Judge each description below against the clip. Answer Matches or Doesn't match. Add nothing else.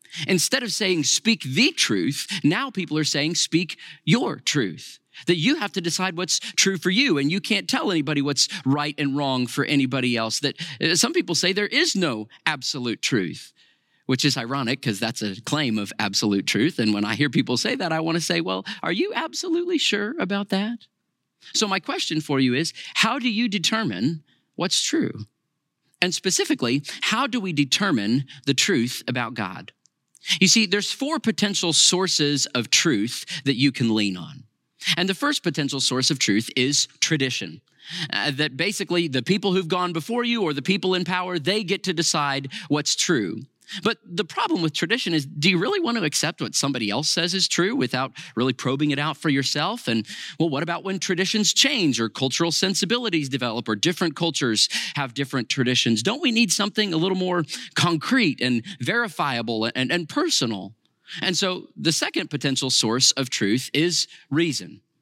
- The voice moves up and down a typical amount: Doesn't match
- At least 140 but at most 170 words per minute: Doesn't match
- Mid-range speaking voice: Matches